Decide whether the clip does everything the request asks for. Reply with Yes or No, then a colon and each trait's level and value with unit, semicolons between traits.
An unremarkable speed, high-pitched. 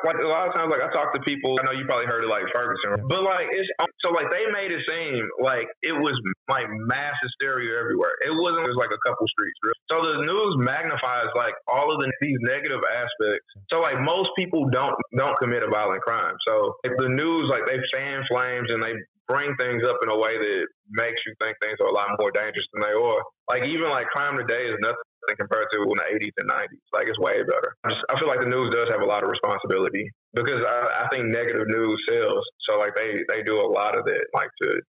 No: fast, 240 wpm; very high, 380 Hz